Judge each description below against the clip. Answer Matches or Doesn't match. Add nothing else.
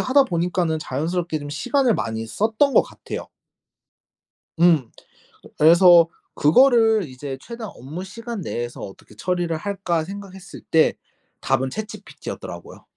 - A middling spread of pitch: Doesn't match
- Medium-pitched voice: Matches